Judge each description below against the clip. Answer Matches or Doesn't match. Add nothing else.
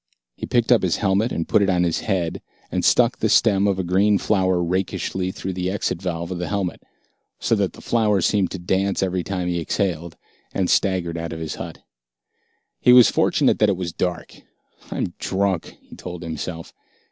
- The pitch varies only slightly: Matches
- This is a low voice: Matches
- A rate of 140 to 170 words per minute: Doesn't match